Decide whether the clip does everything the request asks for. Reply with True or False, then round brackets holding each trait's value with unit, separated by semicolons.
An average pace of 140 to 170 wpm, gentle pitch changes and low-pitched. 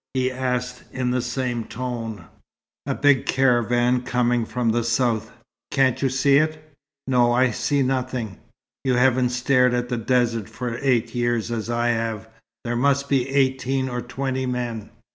True (160 wpm; 1.7 semitones; 125 Hz)